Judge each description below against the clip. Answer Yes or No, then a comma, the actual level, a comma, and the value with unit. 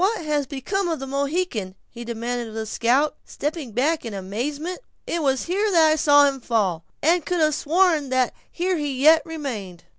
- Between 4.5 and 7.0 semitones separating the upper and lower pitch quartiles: Yes, average, 5.3 semitones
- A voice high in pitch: Yes, very high, 285 Hz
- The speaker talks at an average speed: Yes, average, 190 wpm